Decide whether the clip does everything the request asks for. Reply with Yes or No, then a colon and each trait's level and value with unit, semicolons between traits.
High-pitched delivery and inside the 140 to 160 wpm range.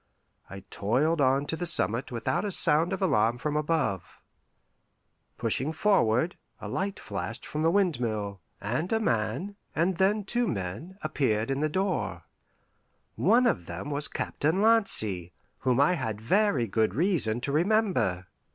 No: medium, 150 Hz; average, 150 wpm